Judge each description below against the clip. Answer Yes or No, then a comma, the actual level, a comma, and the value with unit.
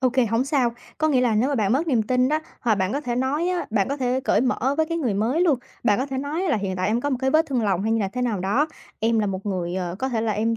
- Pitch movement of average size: Yes, average, 4.5 semitones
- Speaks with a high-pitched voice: Yes, high, 245 Hz